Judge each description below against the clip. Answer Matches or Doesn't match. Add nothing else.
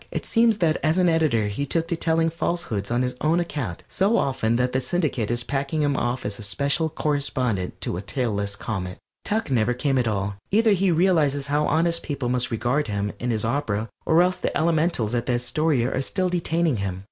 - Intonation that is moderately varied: Doesn't match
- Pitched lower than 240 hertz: Matches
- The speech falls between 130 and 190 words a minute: Doesn't match